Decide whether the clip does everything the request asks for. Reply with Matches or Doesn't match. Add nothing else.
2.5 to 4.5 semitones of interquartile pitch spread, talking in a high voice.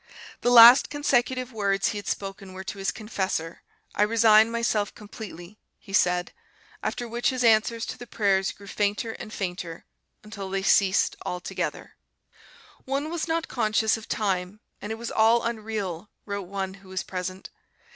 Matches